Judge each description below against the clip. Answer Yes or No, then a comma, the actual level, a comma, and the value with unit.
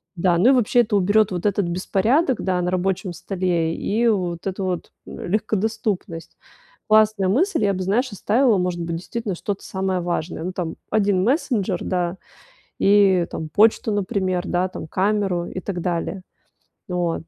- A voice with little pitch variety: No, average, 3.1 semitones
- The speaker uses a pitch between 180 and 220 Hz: Yes, high, 190 Hz